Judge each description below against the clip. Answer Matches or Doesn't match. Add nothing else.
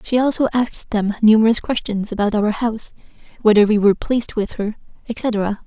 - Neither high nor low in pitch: Doesn't match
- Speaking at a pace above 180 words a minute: Doesn't match